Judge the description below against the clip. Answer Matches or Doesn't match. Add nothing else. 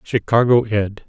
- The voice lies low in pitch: Matches